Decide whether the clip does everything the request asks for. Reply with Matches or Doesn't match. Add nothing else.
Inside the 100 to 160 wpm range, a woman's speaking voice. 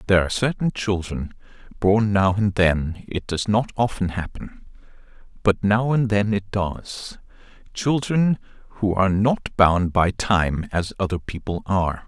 Doesn't match